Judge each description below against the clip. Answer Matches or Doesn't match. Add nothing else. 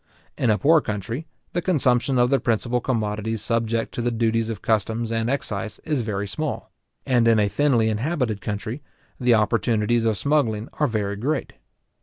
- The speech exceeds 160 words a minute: Matches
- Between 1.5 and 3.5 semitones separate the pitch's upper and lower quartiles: Matches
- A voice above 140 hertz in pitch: Doesn't match